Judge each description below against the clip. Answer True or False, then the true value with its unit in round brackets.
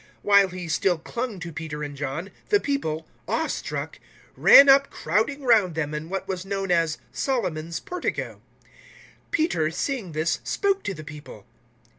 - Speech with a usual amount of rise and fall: False (7.0 semitones)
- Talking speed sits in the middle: True (165 wpm)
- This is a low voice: False (180 Hz)